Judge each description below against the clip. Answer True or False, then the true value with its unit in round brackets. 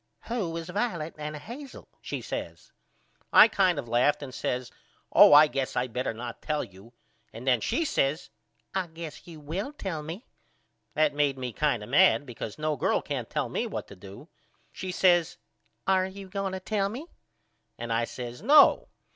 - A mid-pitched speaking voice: True (155 Hz)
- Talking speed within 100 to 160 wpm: False (180 wpm)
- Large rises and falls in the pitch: True (6.8 semitones)